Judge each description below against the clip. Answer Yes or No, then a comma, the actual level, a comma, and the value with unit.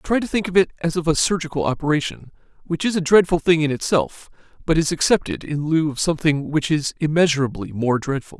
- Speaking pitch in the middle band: Yes, medium, 155 Hz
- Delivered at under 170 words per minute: No, fast, 205 wpm